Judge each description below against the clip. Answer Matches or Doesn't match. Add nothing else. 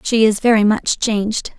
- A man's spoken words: Doesn't match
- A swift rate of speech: Doesn't match